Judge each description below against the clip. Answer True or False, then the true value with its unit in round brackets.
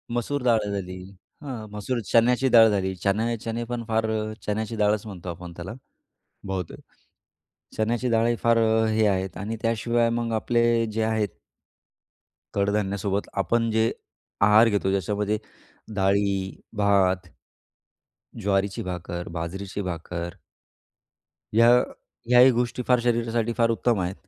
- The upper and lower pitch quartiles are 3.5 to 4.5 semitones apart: False (3.1 semitones)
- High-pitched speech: False (105 Hz)